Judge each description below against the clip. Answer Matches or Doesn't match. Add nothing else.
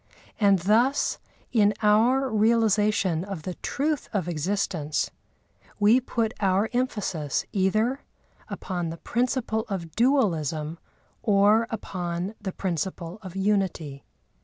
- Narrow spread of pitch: Doesn't match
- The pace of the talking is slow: Matches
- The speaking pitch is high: Matches